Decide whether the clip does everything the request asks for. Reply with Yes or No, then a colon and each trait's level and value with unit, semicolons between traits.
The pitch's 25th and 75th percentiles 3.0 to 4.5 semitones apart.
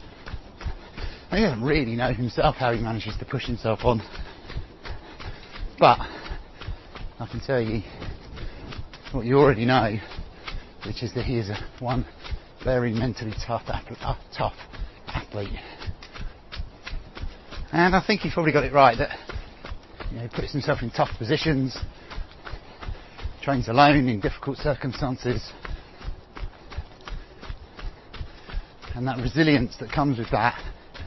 Yes: average, 3.8 semitones